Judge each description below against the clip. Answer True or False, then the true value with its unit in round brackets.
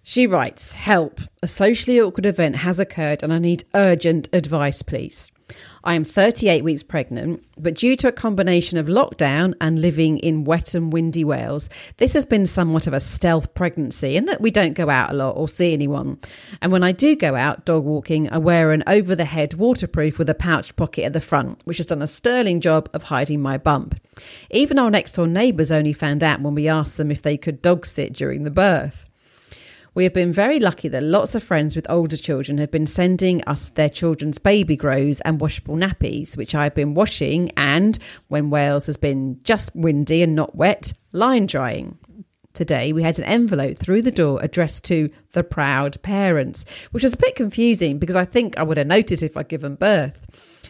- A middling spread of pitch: True (3.8 semitones)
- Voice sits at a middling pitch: True (165 Hz)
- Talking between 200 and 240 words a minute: True (205 wpm)